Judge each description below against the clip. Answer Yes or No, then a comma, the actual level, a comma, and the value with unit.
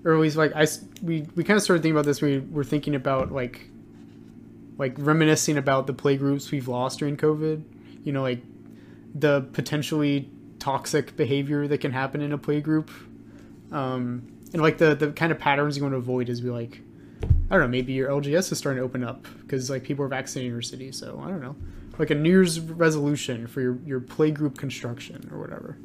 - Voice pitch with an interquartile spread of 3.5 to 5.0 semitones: No, average, 2.9 semitones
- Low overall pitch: No, medium, 145 Hz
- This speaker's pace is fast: Yes, fast, 210 wpm